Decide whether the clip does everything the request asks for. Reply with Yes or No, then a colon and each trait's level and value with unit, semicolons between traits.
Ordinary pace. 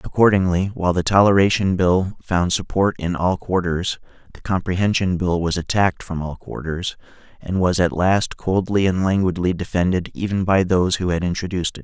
Yes: average, 165 wpm